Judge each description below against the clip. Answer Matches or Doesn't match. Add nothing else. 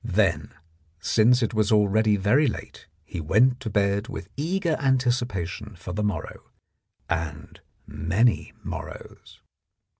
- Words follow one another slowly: Matches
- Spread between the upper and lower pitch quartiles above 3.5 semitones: Matches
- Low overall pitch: Matches